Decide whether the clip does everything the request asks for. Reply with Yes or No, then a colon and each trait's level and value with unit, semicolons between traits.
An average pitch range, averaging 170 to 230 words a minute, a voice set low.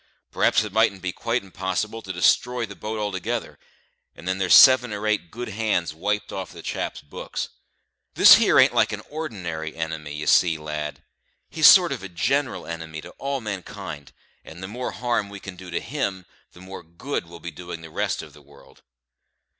Yes: average, 4.9 semitones; average, 195 wpm; very low, 95 Hz